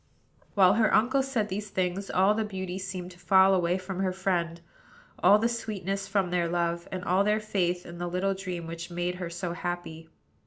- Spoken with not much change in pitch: Yes, narrow, 2.0 semitones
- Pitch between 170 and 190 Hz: Yes, medium, 185 Hz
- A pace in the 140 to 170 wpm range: No, fast, 205 wpm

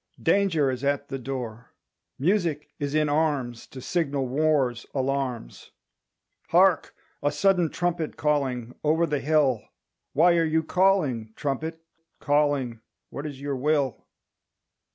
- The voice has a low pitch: No, medium, 145 Hz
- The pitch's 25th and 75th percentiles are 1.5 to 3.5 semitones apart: Yes, average, 3.2 semitones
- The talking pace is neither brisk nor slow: No, slow, 125 wpm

